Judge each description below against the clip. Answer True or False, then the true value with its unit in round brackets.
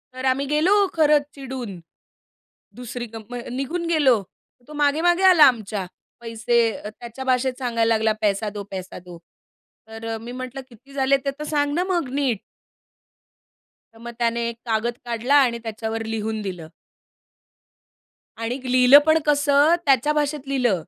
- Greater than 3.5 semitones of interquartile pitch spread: True (4.2 semitones)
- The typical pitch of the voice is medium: False (250 Hz)